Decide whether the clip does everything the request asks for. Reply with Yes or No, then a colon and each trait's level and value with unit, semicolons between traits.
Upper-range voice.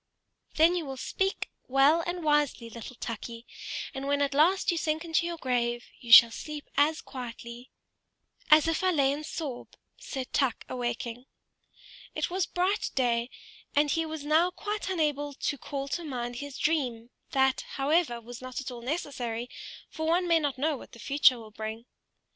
Yes: very high, 280 Hz